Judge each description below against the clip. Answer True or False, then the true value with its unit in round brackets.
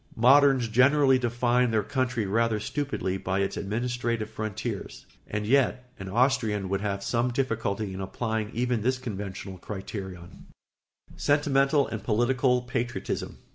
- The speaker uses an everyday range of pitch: True (3.7 semitones)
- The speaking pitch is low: True (115 Hz)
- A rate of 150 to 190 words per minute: False (135 wpm)